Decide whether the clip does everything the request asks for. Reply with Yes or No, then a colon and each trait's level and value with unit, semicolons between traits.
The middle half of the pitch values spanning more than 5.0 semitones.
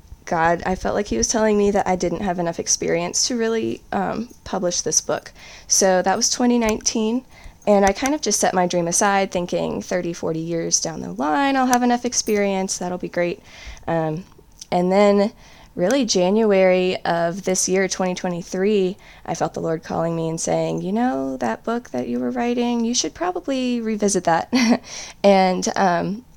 No: average, 4.5 semitones